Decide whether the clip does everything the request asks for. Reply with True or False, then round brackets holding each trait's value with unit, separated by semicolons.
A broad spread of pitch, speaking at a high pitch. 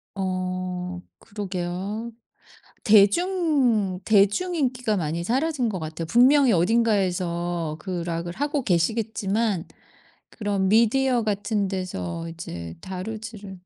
False (4.4 semitones; 200 Hz)